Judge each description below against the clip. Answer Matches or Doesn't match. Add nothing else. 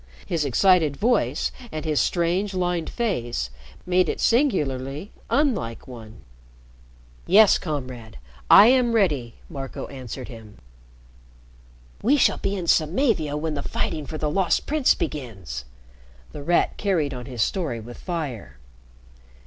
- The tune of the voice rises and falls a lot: Matches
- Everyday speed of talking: Doesn't match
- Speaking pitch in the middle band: Matches